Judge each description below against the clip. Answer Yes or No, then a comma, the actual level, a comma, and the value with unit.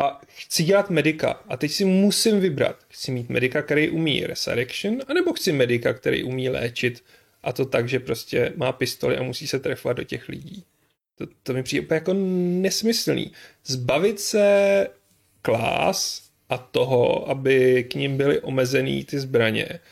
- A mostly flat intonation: No, wide, 6.8 semitones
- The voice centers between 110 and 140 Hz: No, medium, 150 Hz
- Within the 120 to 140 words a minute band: No, average, 165 wpm